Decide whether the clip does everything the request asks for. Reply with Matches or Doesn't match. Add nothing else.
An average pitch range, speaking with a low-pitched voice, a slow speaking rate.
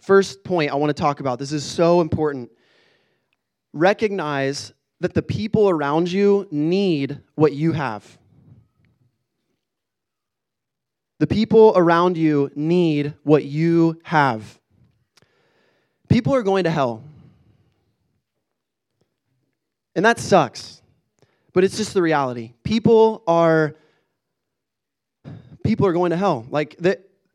Doesn't match